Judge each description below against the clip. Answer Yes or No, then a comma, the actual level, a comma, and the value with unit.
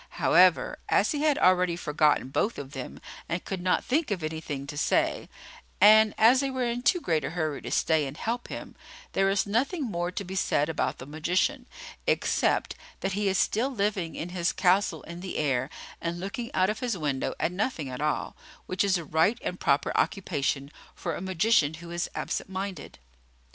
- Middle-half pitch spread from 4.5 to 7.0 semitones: Yes, average, 5.1 semitones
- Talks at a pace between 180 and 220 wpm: Yes, average, 195 wpm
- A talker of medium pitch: Yes, medium, 180 Hz